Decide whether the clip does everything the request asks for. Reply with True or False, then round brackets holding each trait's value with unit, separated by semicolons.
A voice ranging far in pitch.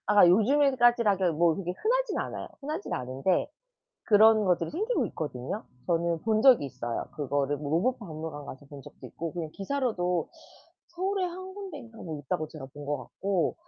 True (8.9 semitones)